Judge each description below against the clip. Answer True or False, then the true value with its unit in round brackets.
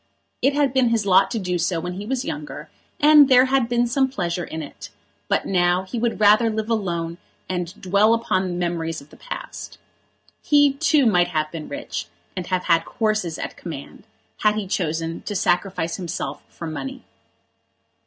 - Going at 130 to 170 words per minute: False (185 wpm)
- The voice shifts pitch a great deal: True (5.7 semitones)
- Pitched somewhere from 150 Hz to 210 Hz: True (190 Hz)